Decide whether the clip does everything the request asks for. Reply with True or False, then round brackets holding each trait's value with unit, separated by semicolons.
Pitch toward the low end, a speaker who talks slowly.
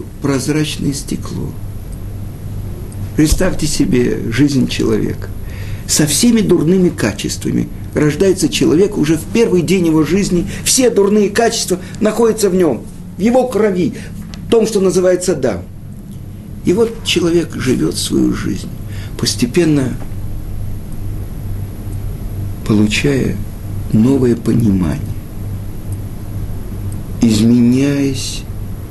True (110 Hz; 90 wpm)